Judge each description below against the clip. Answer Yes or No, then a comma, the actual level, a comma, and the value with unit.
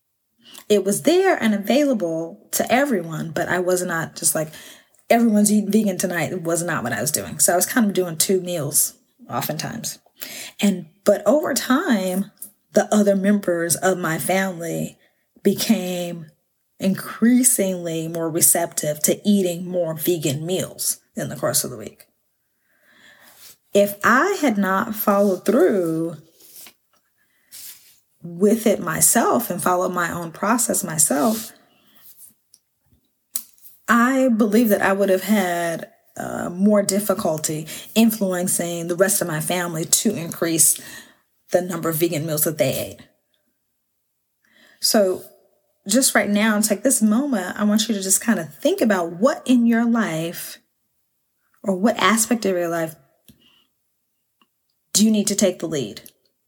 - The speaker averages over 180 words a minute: No, average, 140 wpm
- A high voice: Yes, high, 195 Hz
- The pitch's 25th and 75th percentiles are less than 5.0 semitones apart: Yes, average, 3.9 semitones